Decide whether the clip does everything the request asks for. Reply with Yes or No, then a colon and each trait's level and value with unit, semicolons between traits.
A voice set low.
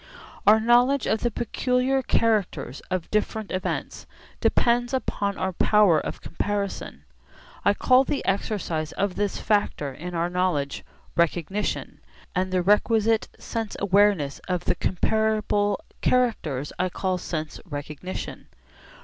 No: high, 200 Hz